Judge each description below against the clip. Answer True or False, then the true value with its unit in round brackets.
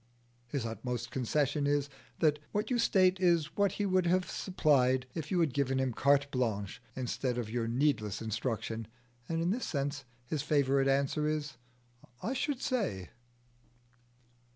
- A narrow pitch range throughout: False (5.3 semitones)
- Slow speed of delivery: False (155 wpm)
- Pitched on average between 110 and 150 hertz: True (140 Hz)